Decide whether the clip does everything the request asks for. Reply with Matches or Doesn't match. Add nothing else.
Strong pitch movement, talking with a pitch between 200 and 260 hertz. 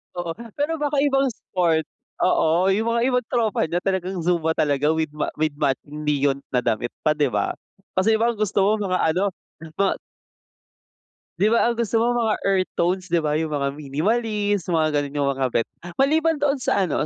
Doesn't match